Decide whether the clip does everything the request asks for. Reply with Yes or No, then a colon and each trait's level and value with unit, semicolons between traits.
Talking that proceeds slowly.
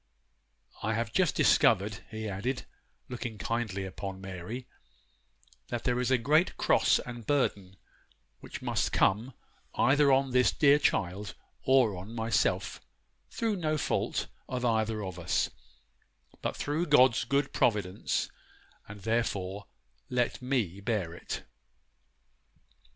Yes: slow, 125 wpm